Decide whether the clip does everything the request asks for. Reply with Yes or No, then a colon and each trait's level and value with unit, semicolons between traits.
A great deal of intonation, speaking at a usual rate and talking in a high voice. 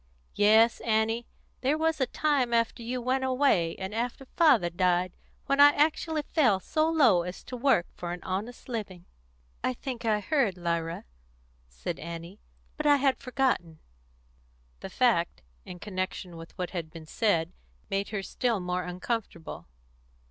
Yes: wide, 6.7 semitones; average, 155 wpm; high, 215 Hz